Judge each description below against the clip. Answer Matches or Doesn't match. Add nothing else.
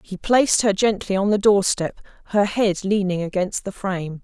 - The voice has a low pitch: Doesn't match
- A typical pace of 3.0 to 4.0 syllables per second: Doesn't match